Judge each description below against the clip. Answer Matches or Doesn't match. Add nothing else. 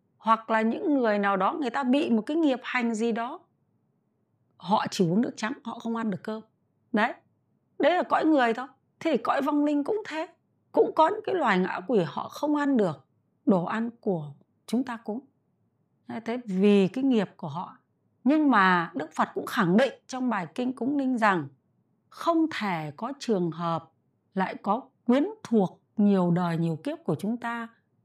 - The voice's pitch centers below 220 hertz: Doesn't match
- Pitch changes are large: Matches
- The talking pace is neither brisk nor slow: Matches